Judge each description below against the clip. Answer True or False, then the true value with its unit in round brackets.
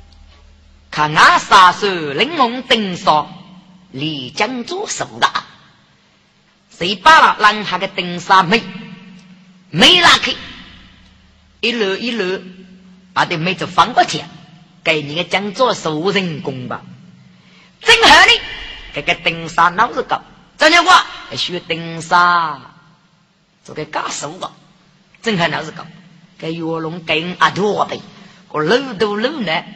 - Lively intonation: False (4.1 semitones)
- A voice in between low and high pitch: True (180 Hz)